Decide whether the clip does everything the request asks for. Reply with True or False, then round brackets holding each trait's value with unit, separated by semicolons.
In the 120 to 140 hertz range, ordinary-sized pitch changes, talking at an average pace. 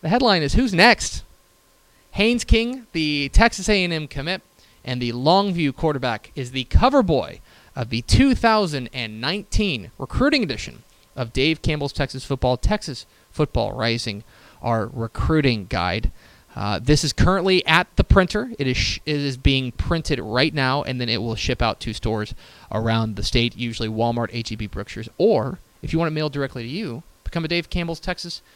False (135 Hz; 6.3 semitones; 170 wpm)